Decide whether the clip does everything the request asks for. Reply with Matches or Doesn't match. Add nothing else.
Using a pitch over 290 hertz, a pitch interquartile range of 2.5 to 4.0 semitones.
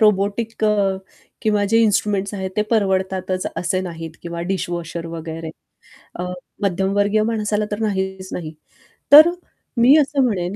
Doesn't match